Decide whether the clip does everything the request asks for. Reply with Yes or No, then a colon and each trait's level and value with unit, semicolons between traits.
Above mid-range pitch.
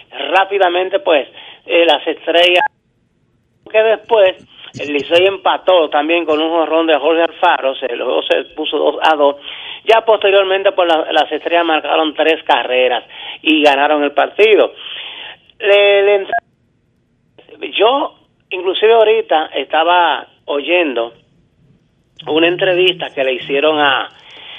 No: medium, 165 Hz